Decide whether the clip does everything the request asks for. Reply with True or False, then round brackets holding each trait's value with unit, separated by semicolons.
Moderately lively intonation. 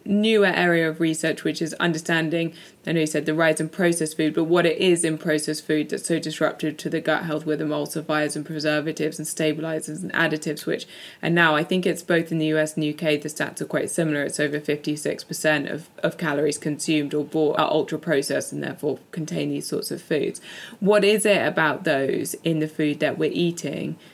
False (1.5 semitones)